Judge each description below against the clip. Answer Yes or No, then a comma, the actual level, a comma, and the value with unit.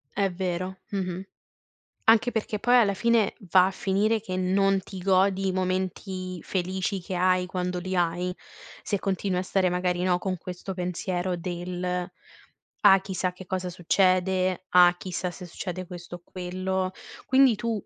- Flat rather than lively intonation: Yes, narrow, 1.2 semitones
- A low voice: No, medium, 185 Hz